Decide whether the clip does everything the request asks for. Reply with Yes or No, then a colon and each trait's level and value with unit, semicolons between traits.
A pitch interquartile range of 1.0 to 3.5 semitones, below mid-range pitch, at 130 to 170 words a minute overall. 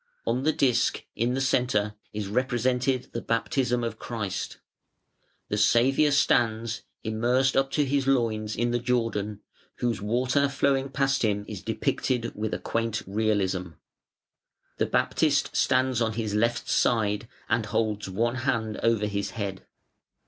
Yes: average, 3.2 semitones; low, 115 Hz; average, 140 wpm